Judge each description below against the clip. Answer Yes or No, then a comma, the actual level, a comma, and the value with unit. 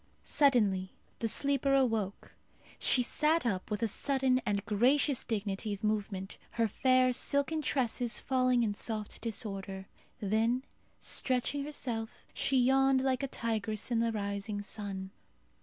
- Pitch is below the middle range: No, high, 230 Hz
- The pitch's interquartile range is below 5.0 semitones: Yes, average, 4.1 semitones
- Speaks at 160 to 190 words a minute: No, slow, 135 wpm